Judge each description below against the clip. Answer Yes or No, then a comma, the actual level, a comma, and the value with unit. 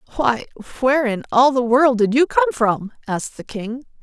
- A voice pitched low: No, very high, 250 Hz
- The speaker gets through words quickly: No, average, 195 wpm